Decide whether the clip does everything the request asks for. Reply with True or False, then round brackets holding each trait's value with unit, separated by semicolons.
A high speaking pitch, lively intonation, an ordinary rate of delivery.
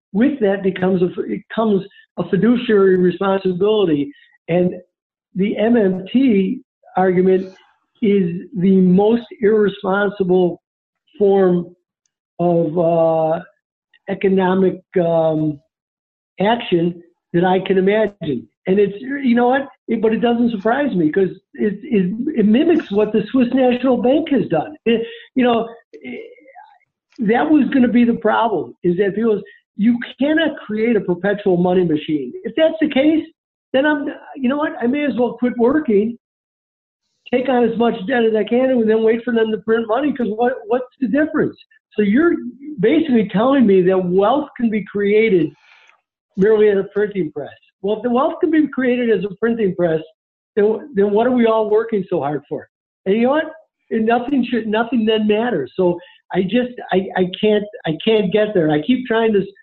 False (220 Hz; 4.8 semitones; 170 wpm)